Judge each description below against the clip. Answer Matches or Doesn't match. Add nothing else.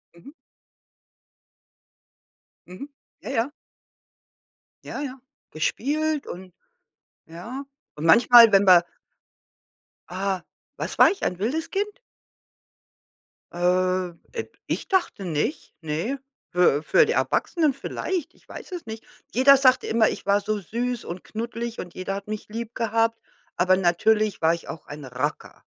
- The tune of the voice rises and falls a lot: Matches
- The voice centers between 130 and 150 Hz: Doesn't match